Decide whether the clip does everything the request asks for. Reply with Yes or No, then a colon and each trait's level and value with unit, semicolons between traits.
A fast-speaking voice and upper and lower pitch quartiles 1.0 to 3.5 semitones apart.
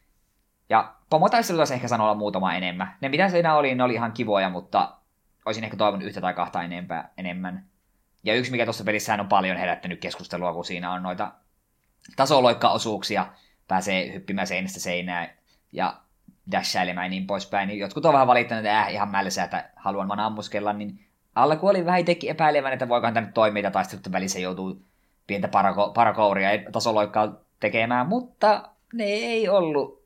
No: fast, 160 wpm; average, 4.7 semitones